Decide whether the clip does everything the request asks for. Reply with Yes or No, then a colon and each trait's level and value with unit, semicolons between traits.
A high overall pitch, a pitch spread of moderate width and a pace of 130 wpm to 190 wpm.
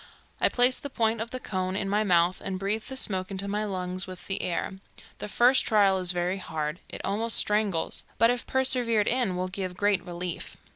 No: high, 195 Hz; average, 3.4 semitones; fast, 205 wpm